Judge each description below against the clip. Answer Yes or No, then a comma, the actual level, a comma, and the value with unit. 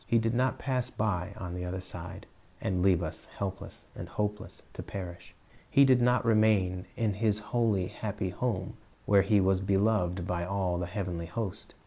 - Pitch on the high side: No, low, 100 Hz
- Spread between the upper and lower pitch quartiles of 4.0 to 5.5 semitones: No, average, 3.4 semitones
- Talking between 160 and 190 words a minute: Yes, average, 180 wpm